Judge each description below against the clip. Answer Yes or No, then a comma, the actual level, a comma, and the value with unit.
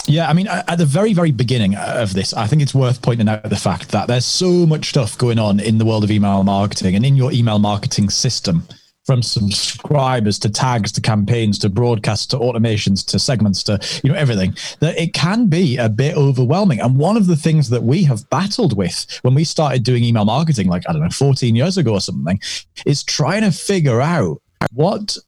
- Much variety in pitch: Yes, wide, 6.4 semitones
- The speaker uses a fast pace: Yes, fast, 215 wpm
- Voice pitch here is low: Yes, low, 125 Hz